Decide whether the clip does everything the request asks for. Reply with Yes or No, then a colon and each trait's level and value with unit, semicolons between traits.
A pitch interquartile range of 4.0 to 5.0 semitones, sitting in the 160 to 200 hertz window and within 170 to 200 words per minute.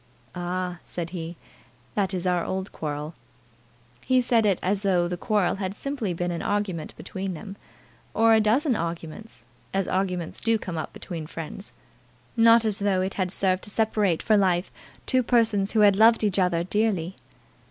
No: average, 3.4 semitones; high, 190 Hz; average, 175 wpm